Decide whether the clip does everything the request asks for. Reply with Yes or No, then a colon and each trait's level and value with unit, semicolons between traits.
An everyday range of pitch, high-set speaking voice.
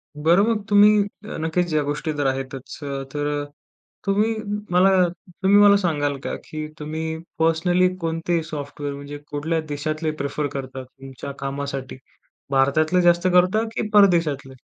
No: average, 4.0 semitones; medium, 155 Hz